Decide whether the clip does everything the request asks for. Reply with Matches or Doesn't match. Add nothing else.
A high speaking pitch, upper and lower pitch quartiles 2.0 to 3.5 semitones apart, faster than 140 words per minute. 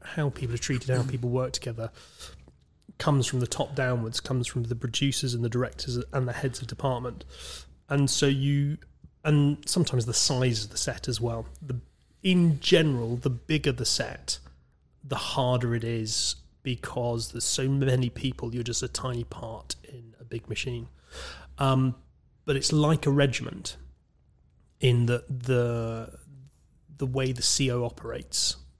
Doesn't match